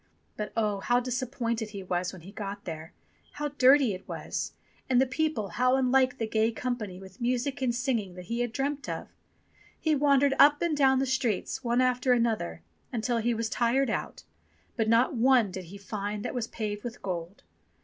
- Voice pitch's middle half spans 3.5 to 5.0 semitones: Yes, average, 4.0 semitones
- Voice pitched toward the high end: Yes, high, 235 Hz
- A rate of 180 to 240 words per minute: Yes, average, 190 wpm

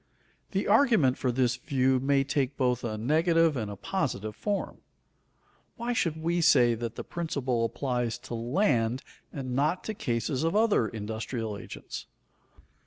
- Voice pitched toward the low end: Yes, low, 130 Hz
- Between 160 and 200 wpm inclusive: No, average, 150 wpm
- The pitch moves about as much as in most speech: No, wide, 5.7 semitones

